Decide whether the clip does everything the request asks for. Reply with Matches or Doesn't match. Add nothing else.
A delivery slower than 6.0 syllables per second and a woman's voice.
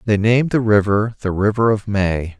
Doesn't match